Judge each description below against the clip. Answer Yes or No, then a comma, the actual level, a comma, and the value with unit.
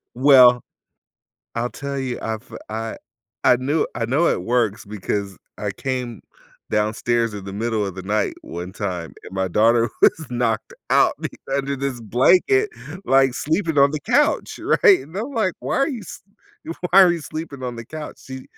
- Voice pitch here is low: Yes, low, 125 Hz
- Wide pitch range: Yes, wide, 5.7 semitones